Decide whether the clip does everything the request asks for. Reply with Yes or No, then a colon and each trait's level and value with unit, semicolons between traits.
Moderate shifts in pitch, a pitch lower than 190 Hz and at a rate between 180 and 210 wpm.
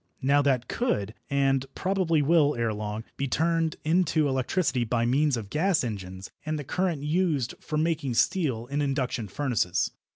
No: average, 5.0 semitones; medium, 140 Hz; average, 160 wpm